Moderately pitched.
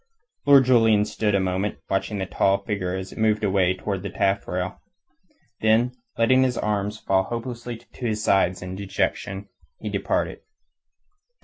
No: low, 100 Hz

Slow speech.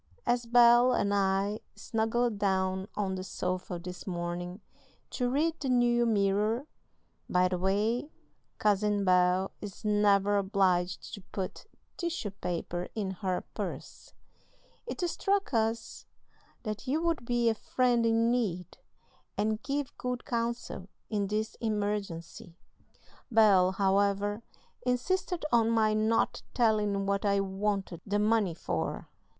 Yes: slow, 125 wpm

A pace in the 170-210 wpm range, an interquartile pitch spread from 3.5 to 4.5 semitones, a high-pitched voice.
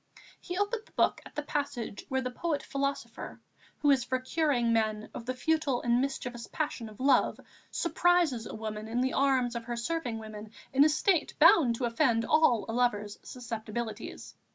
Yes: average, 180 wpm; average, 4.1 semitones; very high, 250 Hz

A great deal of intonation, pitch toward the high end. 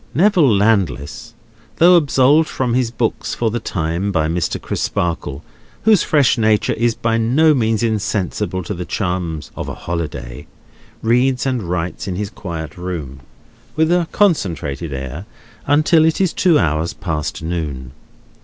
No: wide, 7.8 semitones; low, 105 Hz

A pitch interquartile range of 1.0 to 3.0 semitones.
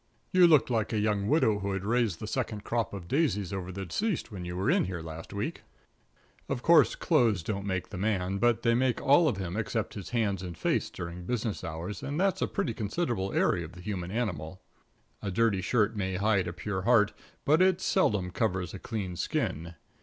No: average, 4.2 semitones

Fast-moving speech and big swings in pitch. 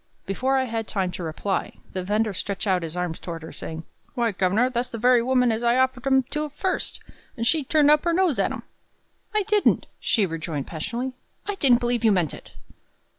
Yes: fast, 210 wpm; wide, 5.8 semitones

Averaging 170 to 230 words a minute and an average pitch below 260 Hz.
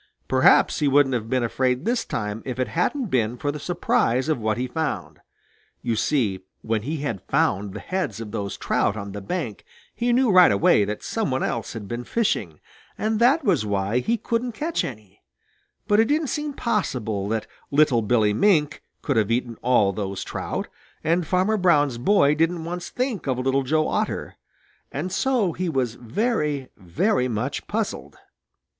Yes: average, 180 wpm; low, 135 Hz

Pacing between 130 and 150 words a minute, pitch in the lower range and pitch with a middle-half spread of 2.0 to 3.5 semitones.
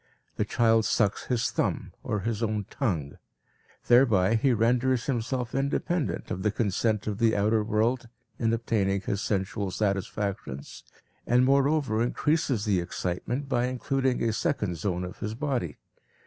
No: average, 145 wpm; low, 115 Hz; average, 3.9 semitones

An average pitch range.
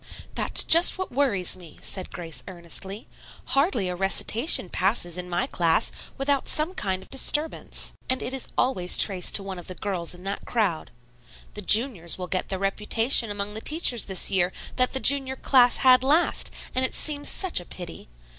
No: wide, 6.4 semitones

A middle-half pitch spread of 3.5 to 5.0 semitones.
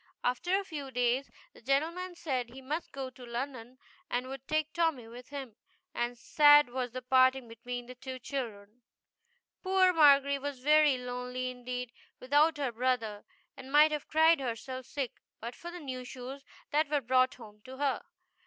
No: average, 2.9 semitones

